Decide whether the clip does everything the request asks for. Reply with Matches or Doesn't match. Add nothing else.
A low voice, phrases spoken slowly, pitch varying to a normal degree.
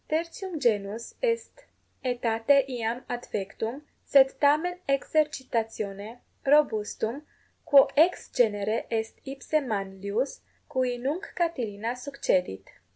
Doesn't match